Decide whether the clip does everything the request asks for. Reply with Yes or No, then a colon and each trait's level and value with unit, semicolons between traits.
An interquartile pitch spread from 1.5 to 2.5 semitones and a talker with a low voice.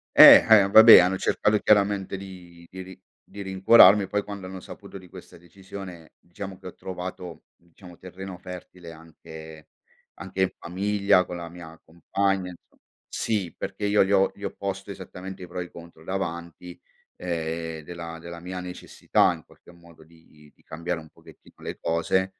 Yes: narrow, 2.2 semitones; very low, 90 Hz